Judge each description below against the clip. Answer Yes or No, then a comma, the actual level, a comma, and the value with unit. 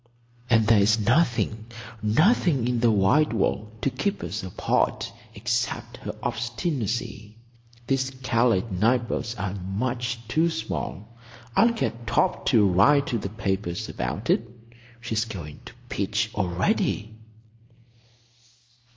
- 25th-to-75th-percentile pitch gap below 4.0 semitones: Yes, average, 3.3 semitones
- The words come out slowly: Yes, slow, 115 wpm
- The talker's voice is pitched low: Yes, low, 115 Hz